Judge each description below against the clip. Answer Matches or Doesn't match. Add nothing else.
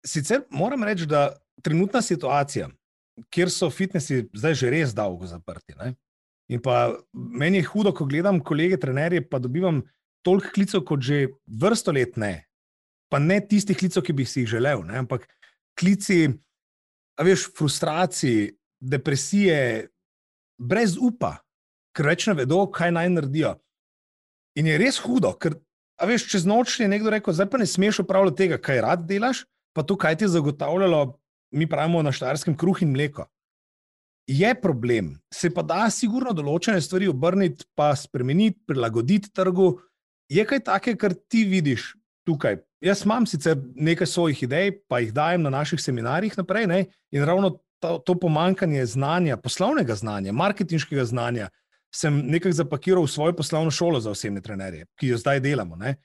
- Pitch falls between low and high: Matches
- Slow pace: Doesn't match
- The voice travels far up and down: Matches